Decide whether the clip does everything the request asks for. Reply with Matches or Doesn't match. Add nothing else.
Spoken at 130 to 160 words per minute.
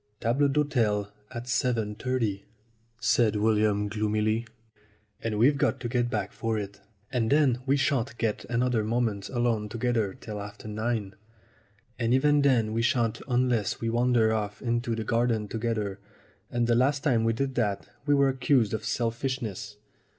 Matches